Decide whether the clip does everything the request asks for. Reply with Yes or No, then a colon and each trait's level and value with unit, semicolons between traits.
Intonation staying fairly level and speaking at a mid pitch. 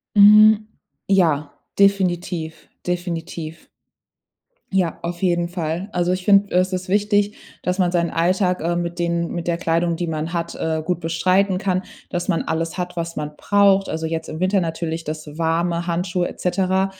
Yes: narrow, 2.0 semitones; medium, 175 Hz